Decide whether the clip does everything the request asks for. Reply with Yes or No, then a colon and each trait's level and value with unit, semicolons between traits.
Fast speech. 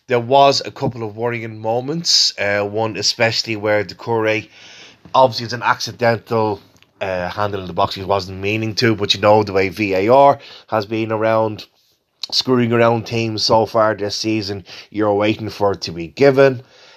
No: average, 175 wpm